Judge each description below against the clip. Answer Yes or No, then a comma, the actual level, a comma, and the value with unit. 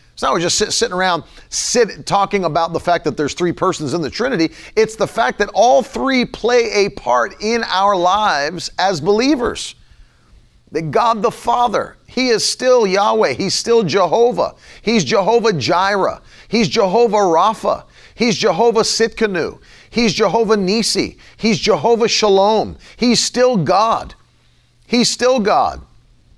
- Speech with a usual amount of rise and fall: Yes, average, 3.4 semitones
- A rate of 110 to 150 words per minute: Yes, average, 145 wpm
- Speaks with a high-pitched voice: Yes, high, 220 Hz